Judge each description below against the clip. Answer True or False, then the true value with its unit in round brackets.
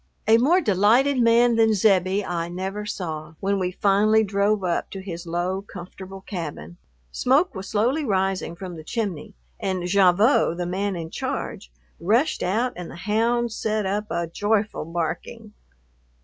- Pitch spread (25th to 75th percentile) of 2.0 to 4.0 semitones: True (3.7 semitones)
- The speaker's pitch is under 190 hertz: False (195 Hz)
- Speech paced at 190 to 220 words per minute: False (155 wpm)